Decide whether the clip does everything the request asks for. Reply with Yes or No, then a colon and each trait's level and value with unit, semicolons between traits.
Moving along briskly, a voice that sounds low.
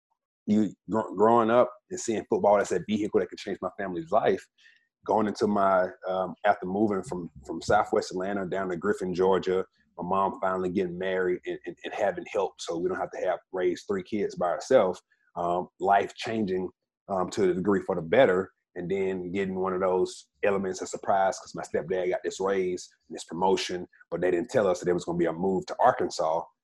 Yes: fast, 210 wpm; very low, 95 Hz